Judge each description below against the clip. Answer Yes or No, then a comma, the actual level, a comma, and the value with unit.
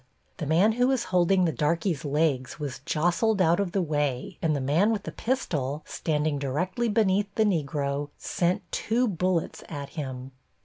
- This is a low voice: No, medium, 165 Hz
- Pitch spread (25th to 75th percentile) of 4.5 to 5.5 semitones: Yes, average, 5.2 semitones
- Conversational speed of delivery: Yes, average, 170 wpm